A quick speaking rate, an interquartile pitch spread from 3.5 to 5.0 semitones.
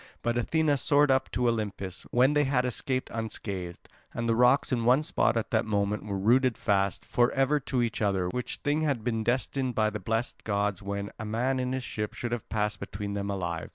Yes: fast, 215 wpm; average, 3.9 semitones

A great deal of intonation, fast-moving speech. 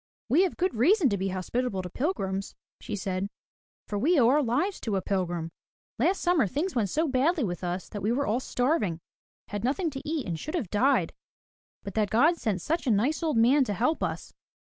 Yes: wide, 7.5 semitones; fast, 215 wpm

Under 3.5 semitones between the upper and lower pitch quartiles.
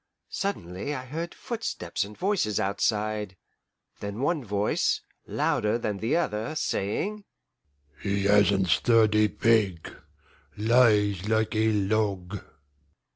Yes: average, 2.8 semitones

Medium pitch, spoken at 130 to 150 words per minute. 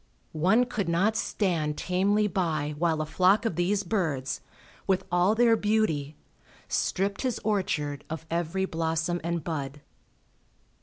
Yes: medium, 175 Hz; slow, 135 wpm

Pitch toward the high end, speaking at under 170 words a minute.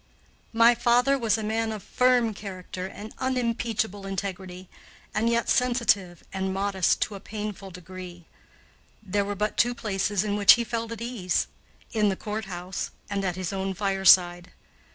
Yes: high, 205 Hz; average, 155 wpm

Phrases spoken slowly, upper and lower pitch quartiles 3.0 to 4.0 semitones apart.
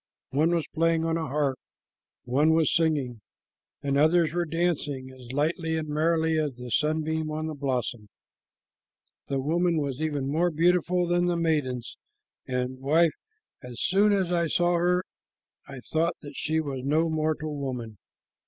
No: average, 155 wpm; average, 3.4 semitones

